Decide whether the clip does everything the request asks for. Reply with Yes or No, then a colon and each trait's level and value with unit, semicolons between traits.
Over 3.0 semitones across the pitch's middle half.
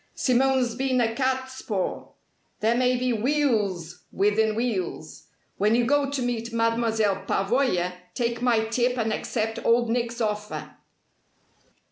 No: average, 2.7 semitones